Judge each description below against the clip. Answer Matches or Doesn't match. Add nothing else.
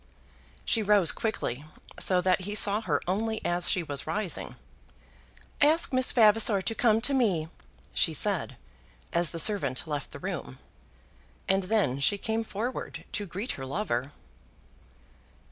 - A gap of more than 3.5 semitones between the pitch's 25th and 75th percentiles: Matches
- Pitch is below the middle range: Doesn't match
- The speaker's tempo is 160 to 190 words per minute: Doesn't match